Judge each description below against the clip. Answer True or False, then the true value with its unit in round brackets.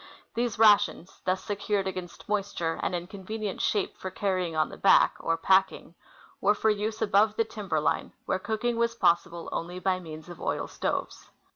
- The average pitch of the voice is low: False (195 Hz)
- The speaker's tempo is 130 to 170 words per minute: False (185 wpm)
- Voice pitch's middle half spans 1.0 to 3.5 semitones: True (3.2 semitones)